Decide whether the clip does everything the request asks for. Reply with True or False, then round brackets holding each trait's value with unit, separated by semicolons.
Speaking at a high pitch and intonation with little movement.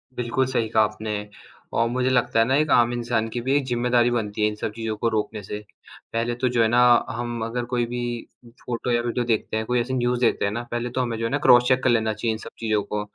False (120 Hz; 1.8 semitones)